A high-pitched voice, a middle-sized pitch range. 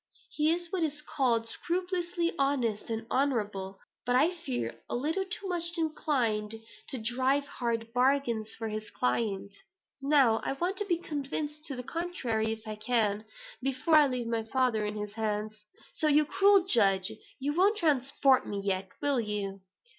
No: very high, 255 Hz; wide, 5.9 semitones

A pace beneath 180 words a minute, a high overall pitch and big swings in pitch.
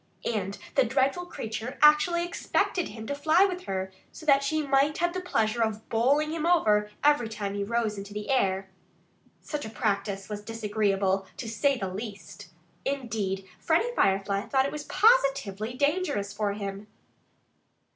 Yes: average, 160 wpm; high, 225 Hz; wide, 6.5 semitones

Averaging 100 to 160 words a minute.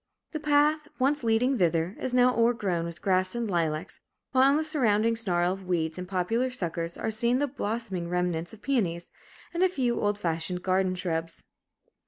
No: average, 180 wpm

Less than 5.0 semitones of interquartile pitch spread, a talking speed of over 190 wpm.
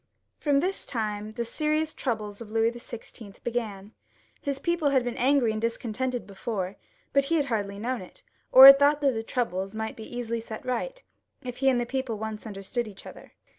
Yes: average, 3.8 semitones; average, 200 wpm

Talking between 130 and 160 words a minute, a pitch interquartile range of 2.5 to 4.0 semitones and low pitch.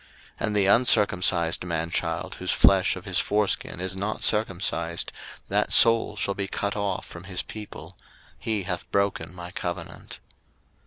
Yes: average, 155 wpm; average, 3.0 semitones; very low, 95 Hz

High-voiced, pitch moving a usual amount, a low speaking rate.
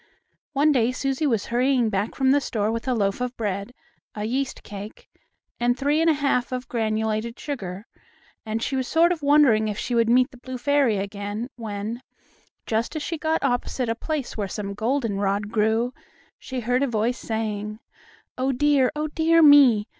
No: high, 240 Hz; average, 4.2 semitones; average, 185 wpm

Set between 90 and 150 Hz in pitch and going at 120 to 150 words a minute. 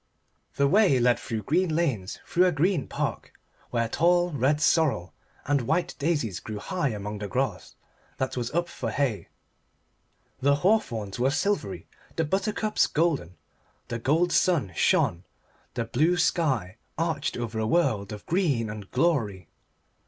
Yes: medium, 140 Hz; average, 145 wpm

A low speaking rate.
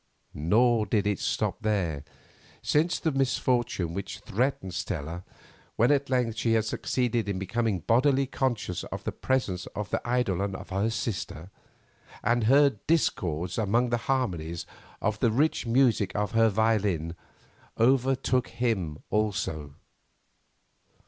Yes: slow, 130 wpm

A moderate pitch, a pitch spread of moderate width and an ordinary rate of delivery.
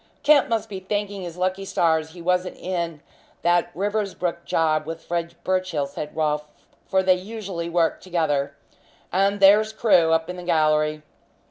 Yes: medium, 175 Hz; average, 3.1 semitones; average, 155 wpm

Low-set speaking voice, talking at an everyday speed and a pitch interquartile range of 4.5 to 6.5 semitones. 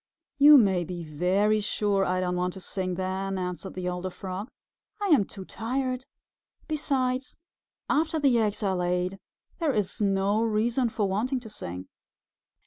No: high, 200 Hz; average, 155 wpm; average, 5.1 semitones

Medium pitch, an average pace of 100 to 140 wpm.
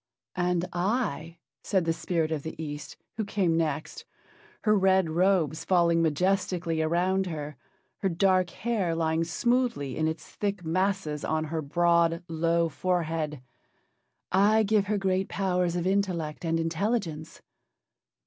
Yes: medium, 170 Hz; slow, 135 wpm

